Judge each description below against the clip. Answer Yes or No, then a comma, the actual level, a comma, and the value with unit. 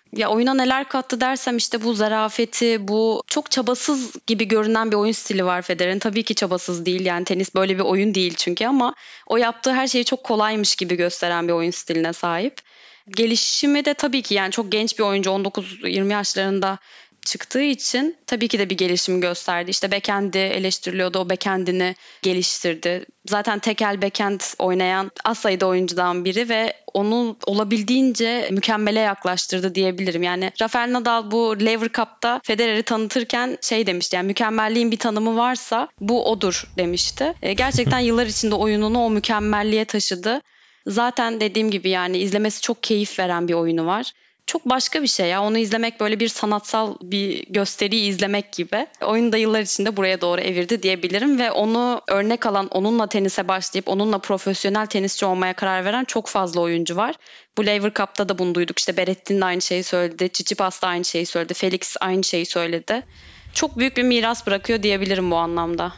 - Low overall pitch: No, high, 205 Hz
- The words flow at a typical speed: No, fast, 165 wpm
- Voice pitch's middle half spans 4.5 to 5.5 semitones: No, average, 3.5 semitones